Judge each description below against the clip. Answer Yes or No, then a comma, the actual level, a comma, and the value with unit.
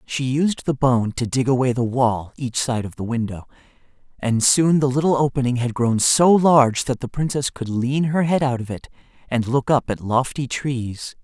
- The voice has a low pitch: Yes, low, 130 Hz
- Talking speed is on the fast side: Yes, fast, 210 wpm